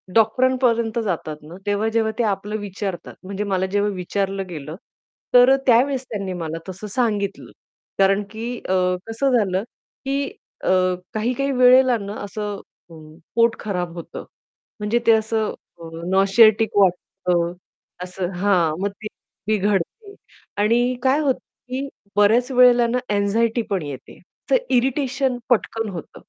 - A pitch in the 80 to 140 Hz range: No, high, 210 Hz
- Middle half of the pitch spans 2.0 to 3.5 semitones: No, average, 3.9 semitones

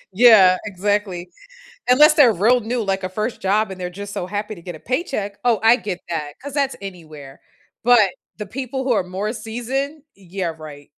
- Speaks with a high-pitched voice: Yes, high, 205 Hz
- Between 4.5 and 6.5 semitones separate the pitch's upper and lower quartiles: Yes, average, 5.0 semitones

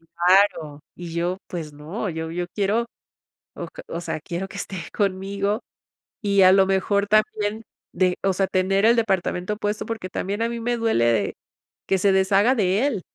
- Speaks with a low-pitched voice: No, high, 195 Hz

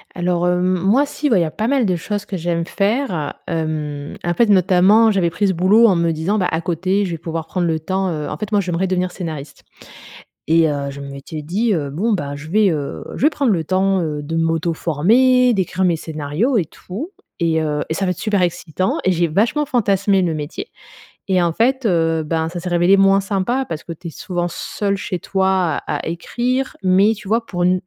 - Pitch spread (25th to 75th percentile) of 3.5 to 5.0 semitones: Yes, average, 3.8 semitones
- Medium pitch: Yes, medium, 180 Hz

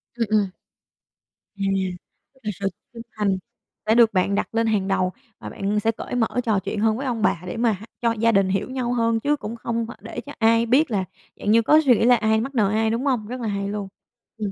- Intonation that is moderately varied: No, narrow, 2.3 semitones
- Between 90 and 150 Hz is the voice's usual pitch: No, high, 225 Hz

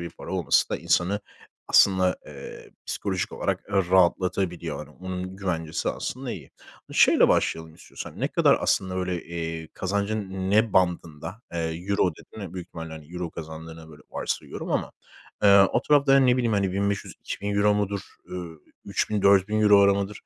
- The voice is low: Yes, very low, 95 Hz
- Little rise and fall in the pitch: No, average, 3.1 semitones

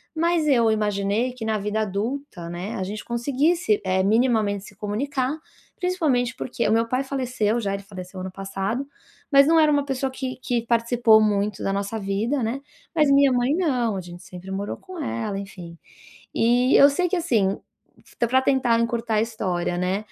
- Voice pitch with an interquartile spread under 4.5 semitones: No, average, 4.8 semitones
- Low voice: No, high, 230 Hz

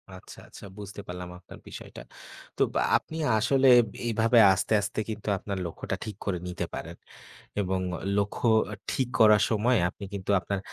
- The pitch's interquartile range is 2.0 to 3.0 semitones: Yes, average, 2.7 semitones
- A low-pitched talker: Yes, low, 105 Hz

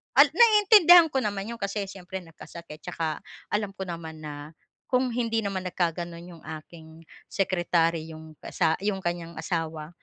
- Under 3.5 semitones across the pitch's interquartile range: No, average, 4.3 semitones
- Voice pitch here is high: No, medium, 180 Hz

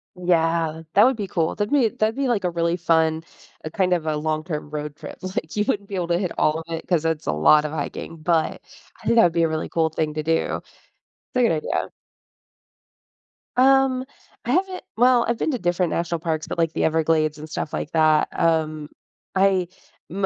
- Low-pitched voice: No, medium, 165 Hz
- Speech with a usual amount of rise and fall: Yes, average, 3.8 semitones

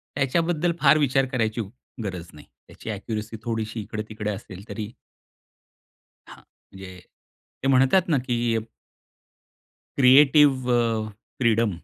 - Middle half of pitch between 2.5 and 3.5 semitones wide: No, average, 4.1 semitones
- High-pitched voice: No, low, 115 Hz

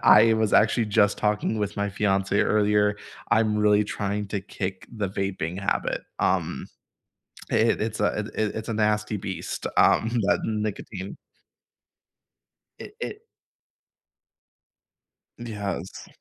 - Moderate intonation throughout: No, narrow, 1.3 semitones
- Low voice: Yes, low, 105 Hz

